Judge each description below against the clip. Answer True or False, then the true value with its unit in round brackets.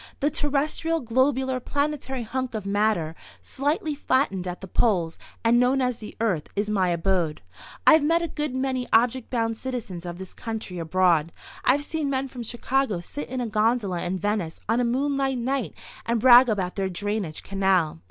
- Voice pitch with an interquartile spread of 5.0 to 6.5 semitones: True (5.6 semitones)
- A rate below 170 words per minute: False (175 wpm)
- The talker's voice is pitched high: True (230 Hz)